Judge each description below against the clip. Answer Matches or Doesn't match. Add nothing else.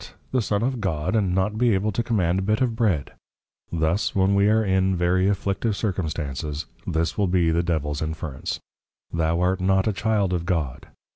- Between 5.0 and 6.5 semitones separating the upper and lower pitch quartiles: Doesn't match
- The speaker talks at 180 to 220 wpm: Matches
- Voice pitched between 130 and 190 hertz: Doesn't match